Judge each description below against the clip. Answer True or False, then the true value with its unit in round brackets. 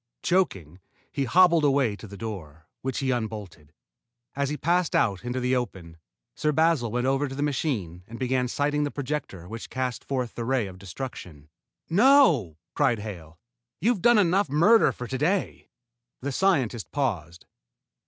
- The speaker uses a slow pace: False (165 wpm)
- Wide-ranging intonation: True (6.4 semitones)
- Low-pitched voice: True (130 Hz)